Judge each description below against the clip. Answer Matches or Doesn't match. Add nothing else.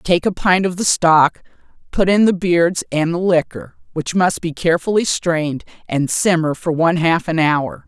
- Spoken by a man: Doesn't match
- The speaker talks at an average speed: Matches